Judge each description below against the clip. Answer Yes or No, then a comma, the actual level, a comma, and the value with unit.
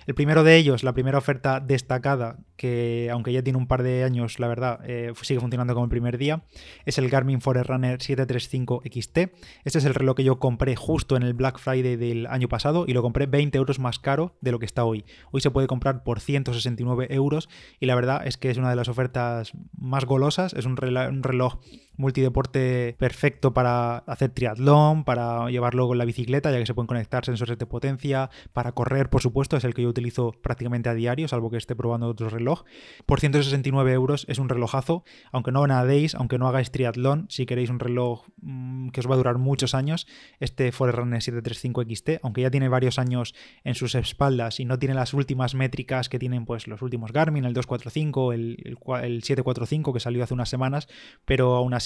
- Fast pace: Yes, fast, 205 wpm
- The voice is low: Yes, low, 130 Hz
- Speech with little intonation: Yes, narrow, 1.9 semitones